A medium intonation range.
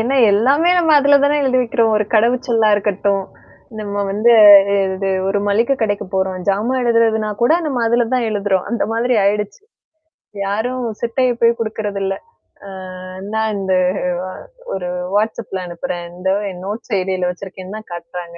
Yes: average, 3.4 semitones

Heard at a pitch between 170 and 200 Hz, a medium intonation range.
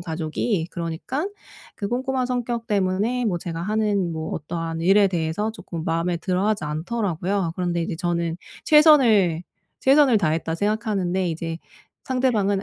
Yes: high, 190 Hz; average, 4.9 semitones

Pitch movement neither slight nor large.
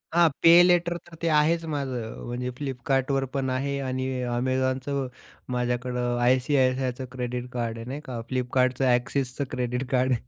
No: narrow, 1.9 semitones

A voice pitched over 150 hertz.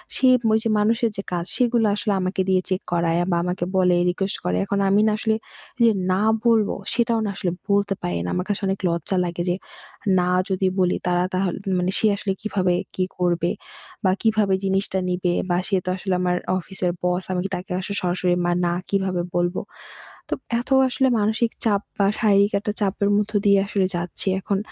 Yes: high, 190 Hz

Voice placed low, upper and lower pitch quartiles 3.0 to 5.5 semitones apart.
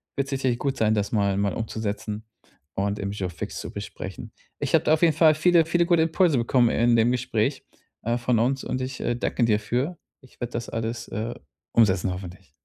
Yes: low, 120 Hz; average, 4.5 semitones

